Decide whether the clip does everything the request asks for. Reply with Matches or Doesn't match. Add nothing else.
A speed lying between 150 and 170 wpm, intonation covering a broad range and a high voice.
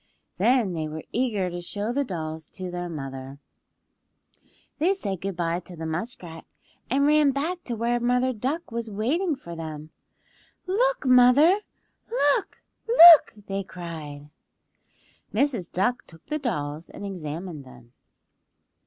Doesn't match